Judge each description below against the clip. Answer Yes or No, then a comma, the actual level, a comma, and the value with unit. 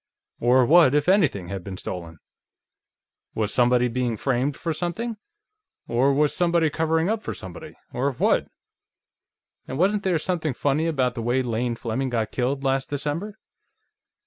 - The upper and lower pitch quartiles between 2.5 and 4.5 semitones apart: No, average, 5.2 semitones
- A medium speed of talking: Yes, average, 150 wpm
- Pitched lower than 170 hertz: Yes, low, 135 Hz